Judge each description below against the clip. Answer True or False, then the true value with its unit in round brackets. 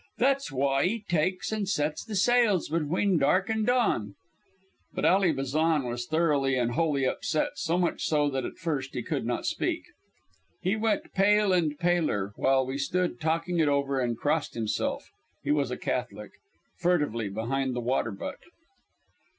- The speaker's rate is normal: True (165 wpm)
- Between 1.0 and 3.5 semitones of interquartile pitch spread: False (5.5 semitones)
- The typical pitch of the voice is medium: True (150 Hz)